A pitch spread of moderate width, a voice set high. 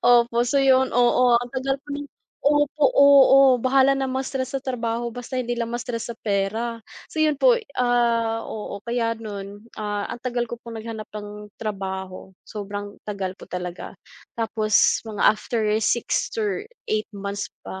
Yes: average, 3.7 semitones; high, 235 Hz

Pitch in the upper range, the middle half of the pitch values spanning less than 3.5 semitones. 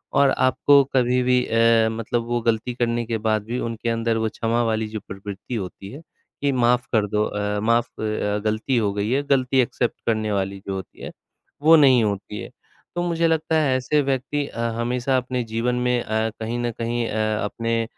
No: low, 115 Hz; narrow, 2.4 semitones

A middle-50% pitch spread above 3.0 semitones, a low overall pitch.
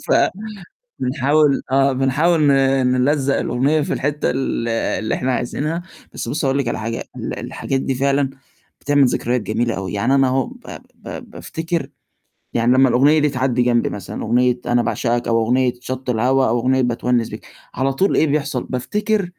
No: narrow, 2.5 semitones; low, 130 Hz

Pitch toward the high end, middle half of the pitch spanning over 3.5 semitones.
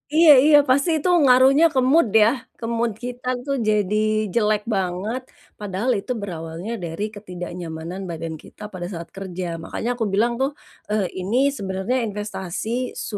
Yes: high, 210 Hz; wide, 5.4 semitones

